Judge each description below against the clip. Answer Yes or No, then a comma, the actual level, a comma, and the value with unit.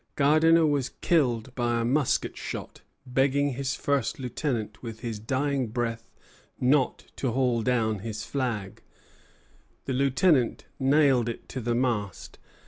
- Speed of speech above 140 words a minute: No, slow, 135 wpm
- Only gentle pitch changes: No, average, 3.1 semitones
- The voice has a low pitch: Yes, low, 125 Hz